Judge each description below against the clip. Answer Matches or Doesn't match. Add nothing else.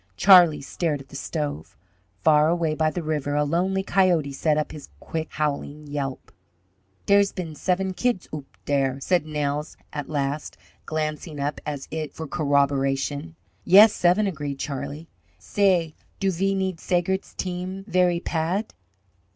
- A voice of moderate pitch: Matches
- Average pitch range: Matches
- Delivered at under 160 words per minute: Matches